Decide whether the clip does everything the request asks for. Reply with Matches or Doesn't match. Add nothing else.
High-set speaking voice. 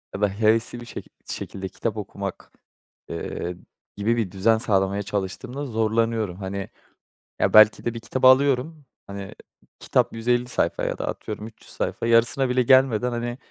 Doesn't match